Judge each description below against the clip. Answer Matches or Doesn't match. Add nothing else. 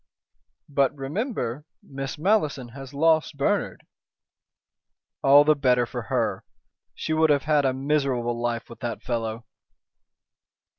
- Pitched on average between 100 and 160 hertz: Matches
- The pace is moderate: Doesn't match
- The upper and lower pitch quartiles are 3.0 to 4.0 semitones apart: Matches